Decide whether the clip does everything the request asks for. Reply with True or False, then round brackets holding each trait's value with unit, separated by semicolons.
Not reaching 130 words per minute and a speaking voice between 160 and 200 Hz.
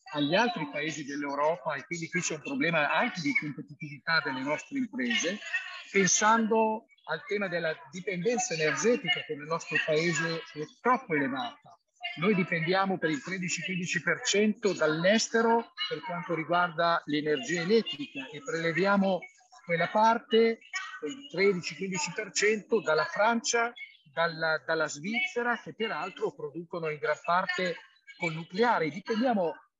True (120 wpm; 185 Hz)